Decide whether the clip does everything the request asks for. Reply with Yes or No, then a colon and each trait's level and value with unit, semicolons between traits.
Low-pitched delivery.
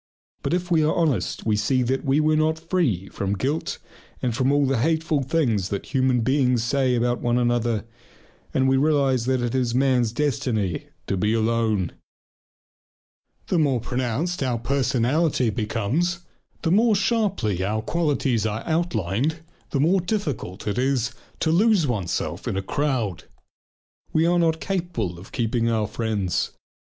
Yes: low, 130 Hz